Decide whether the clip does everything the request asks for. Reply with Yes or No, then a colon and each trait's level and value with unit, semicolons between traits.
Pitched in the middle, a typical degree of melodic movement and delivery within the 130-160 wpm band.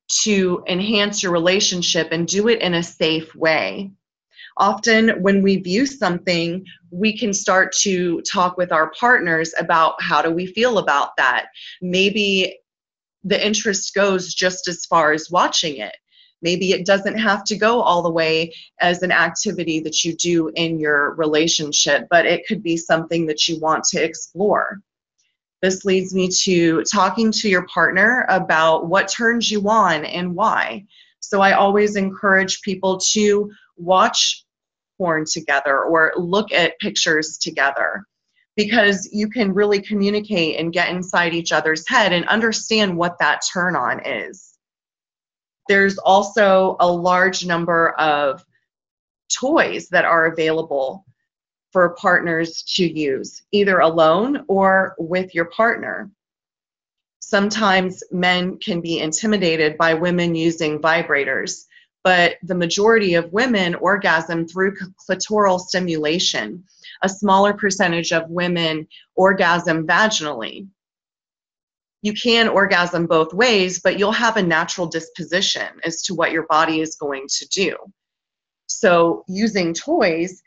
Yes: medium, 180 Hz; average, 3.3 semitones; slow, 135 wpm